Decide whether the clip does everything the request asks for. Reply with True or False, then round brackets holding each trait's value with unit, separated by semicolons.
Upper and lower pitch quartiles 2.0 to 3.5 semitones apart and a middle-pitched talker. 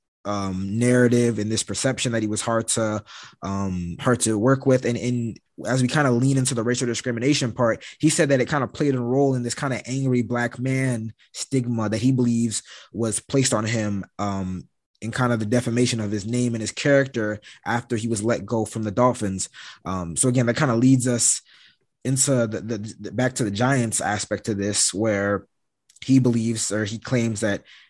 False (2.8 semitones; 120 Hz)